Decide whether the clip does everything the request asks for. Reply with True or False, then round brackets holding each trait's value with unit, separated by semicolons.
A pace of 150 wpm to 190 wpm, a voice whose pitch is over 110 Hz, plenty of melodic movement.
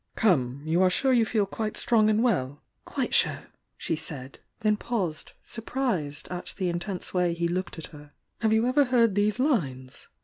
True (175 wpm; 185 Hz; 6.2 semitones)